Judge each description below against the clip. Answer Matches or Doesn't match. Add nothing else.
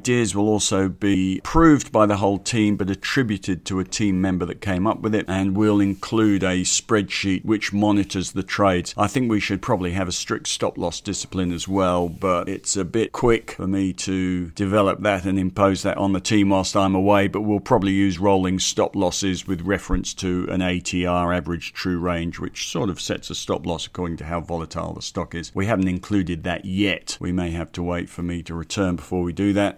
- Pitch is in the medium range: Doesn't match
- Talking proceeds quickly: Matches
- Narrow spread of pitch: Matches